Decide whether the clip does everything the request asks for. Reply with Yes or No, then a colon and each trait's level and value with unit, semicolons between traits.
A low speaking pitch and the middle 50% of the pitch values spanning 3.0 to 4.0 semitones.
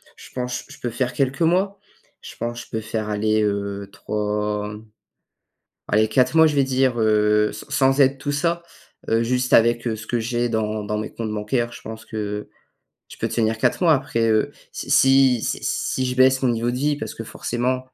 Yes: low, 120 Hz; average, 3.4 semitones